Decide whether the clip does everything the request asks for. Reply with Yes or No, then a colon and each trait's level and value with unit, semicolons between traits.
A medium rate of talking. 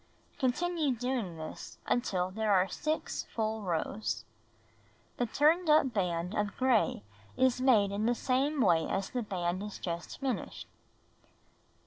No: slow, 130 wpm